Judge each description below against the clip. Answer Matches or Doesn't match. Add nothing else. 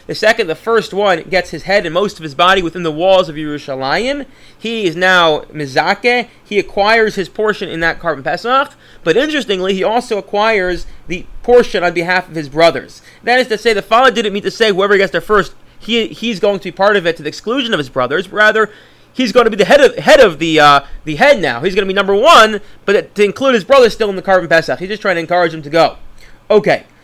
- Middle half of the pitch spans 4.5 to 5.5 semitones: Matches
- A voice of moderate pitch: Doesn't match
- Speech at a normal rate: Doesn't match